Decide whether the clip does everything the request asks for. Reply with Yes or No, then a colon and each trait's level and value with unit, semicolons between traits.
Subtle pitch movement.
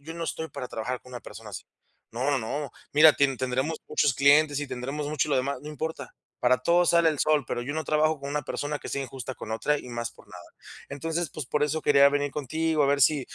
No: average, 3.0 semitones